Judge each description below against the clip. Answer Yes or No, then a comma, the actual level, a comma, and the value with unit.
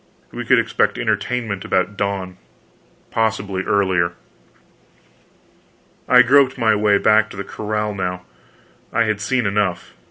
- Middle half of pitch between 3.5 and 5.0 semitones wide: No, narrow, 2.4 semitones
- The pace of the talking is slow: Yes, slow, 125 wpm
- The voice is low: Yes, low, 105 Hz